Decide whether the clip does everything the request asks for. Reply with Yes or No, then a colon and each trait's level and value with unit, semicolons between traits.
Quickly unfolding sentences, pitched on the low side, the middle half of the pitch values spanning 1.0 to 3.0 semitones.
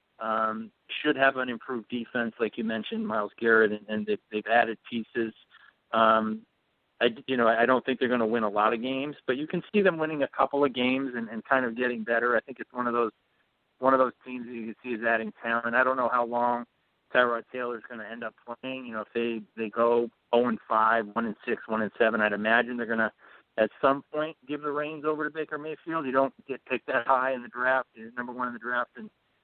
Yes: fast, 255 wpm; low, 120 Hz; average, 2.7 semitones